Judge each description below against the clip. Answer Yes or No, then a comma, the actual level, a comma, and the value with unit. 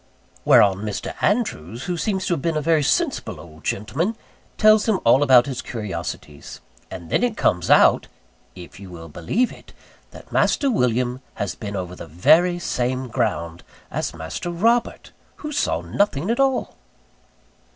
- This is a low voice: Yes, low, 125 Hz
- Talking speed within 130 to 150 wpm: No, average, 160 wpm